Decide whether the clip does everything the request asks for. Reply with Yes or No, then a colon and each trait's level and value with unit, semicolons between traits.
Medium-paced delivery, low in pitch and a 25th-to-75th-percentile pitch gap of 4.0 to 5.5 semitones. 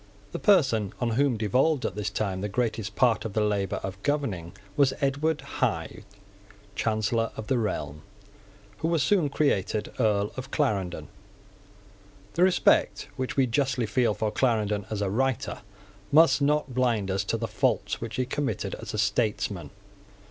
Yes: average, 160 wpm; low, 115 Hz; average, 4.6 semitones